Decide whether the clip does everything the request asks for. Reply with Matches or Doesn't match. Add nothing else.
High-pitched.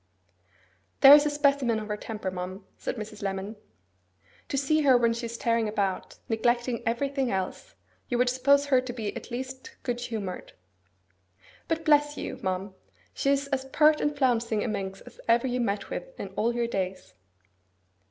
Matches